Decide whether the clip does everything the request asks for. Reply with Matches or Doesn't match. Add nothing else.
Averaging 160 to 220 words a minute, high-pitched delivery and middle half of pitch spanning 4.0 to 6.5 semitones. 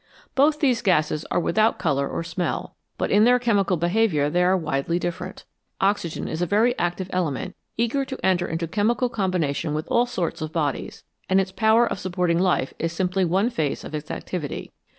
Doesn't match